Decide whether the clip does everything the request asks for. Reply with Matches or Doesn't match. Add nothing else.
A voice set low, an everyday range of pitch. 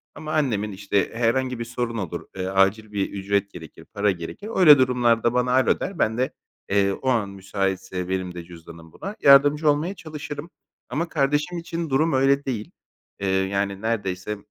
Doesn't match